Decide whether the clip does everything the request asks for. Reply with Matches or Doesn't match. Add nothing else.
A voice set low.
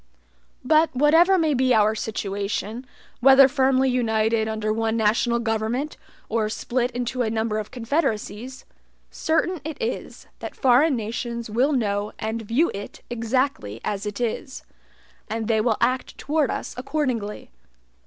Doesn't match